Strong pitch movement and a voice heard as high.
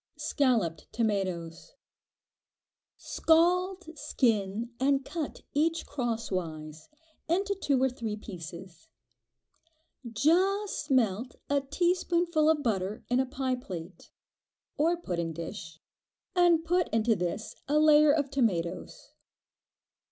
Yes: wide, 8.8 semitones; very high, 255 Hz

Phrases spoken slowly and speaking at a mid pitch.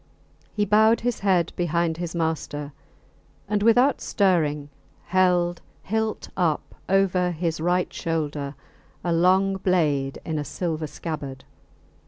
Yes: slow, 120 wpm; medium, 175 Hz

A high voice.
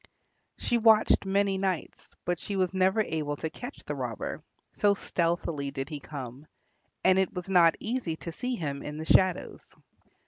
No: medium, 180 Hz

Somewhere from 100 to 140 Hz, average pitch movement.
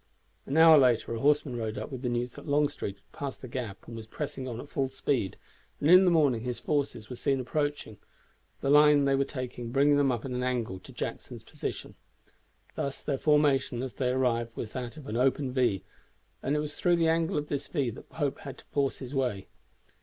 Yes: low, 135 Hz; average, 3.3 semitones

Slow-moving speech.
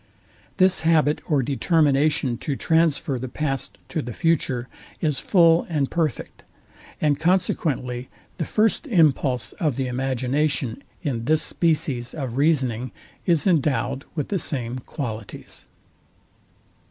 Yes: slow, 120 wpm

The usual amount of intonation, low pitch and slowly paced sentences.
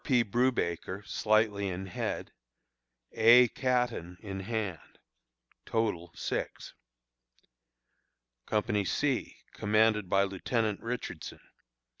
Yes: average, 3.4 semitones; low, 105 Hz; slow, 85 wpm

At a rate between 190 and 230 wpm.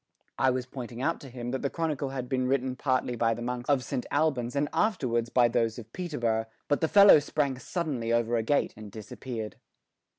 Yes: fast, 205 wpm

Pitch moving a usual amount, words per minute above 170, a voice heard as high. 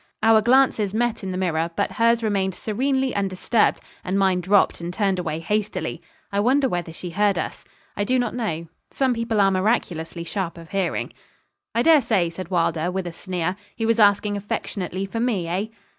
Yes: average, 4.0 semitones; average, 190 wpm; high, 195 Hz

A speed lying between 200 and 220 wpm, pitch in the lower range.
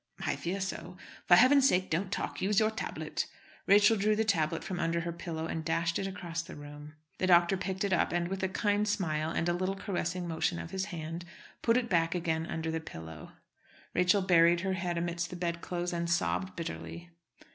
No: fast, 205 wpm; medium, 175 Hz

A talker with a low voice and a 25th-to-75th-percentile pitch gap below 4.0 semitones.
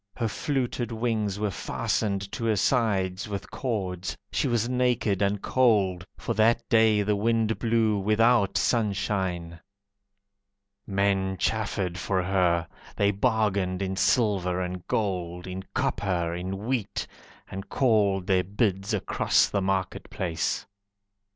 Yes: low, 100 Hz; average, 3.0 semitones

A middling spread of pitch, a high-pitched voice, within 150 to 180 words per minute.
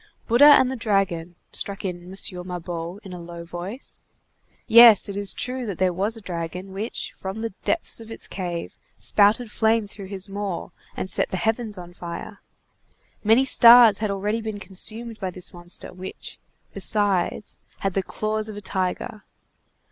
Yes: average, 3.4 semitones; high, 200 Hz; average, 170 wpm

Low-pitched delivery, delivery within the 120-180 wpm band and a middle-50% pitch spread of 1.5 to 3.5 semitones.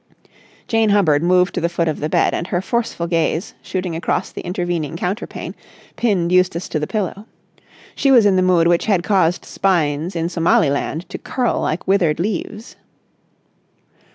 No: medium, 180 Hz; average, 165 wpm; average, 2.9 semitones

